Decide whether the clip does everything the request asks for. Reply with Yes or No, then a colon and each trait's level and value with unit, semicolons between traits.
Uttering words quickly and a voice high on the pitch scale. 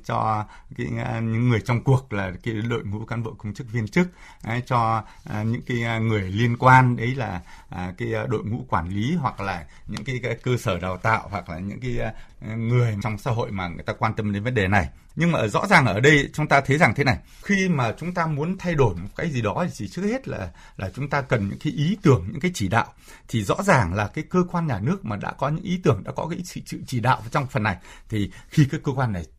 No: fast, 260 wpm; low, 120 Hz